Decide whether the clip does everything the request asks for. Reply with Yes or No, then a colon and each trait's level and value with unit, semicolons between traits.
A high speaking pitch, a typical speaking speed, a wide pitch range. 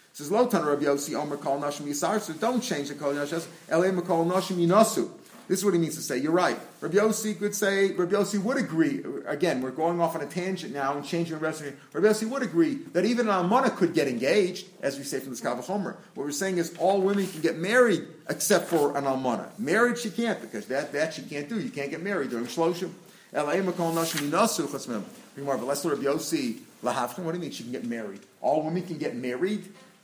No: medium, 180 Hz; average, 175 wpm; wide, 5.7 semitones